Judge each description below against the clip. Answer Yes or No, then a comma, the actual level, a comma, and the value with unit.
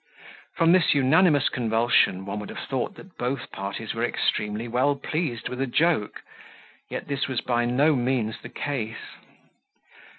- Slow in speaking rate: No, average, 155 wpm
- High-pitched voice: No, low, 125 Hz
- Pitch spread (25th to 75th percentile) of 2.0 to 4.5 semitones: Yes, average, 4.0 semitones